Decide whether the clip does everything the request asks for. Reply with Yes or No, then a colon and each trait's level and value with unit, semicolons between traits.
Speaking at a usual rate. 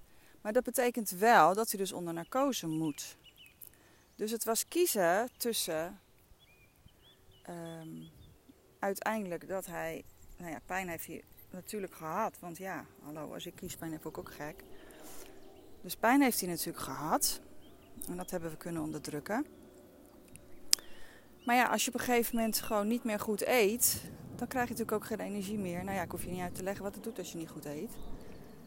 Yes: average, 180 wpm